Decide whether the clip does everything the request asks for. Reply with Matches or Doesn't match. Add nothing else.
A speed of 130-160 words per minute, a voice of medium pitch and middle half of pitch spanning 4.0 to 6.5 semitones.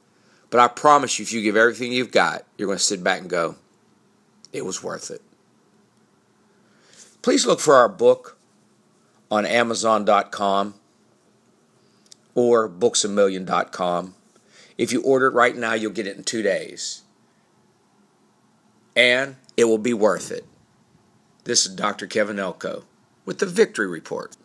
Doesn't match